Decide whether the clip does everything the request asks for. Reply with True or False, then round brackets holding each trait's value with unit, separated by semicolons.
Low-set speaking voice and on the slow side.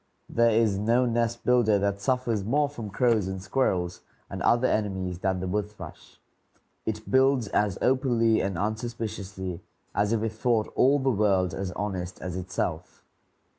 False (105 Hz; 160 wpm)